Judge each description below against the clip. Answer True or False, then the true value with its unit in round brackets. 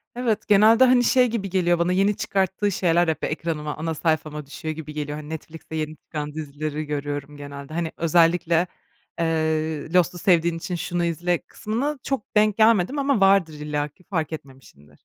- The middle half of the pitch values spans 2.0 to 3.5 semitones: False (4.2 semitones)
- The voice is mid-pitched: True (165 Hz)